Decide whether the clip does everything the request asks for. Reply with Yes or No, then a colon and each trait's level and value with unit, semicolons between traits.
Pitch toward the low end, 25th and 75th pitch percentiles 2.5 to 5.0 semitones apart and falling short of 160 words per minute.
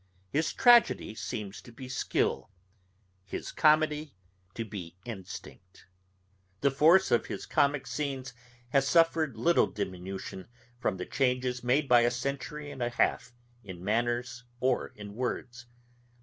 Yes: low, 125 Hz; average, 4.6 semitones; slow, 135 wpm